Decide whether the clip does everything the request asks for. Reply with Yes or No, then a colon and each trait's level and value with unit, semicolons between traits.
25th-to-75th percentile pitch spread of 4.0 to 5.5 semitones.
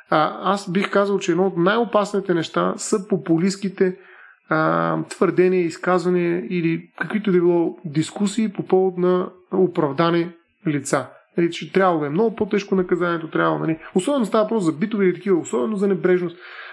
No: narrow, 2.6 semitones